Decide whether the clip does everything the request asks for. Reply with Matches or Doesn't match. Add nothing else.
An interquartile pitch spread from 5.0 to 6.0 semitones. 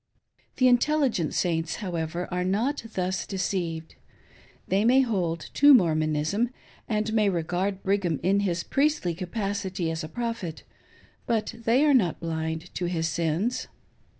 Matches